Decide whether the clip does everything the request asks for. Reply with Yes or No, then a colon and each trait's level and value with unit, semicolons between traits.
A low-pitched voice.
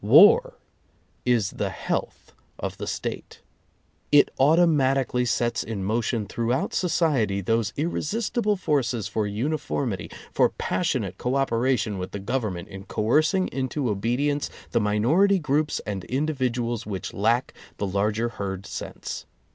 Yes: low, 120 Hz